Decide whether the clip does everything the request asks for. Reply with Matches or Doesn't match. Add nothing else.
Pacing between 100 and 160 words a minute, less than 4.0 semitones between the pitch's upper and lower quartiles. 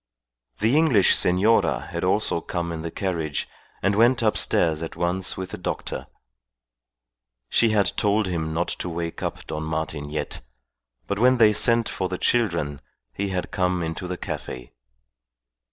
Doesn't match